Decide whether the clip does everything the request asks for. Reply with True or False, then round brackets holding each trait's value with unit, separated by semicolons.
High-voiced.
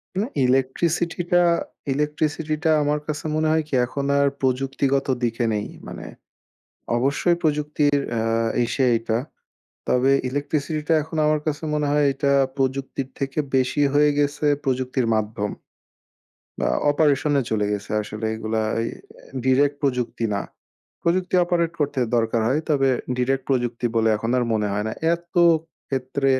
False (140 Hz)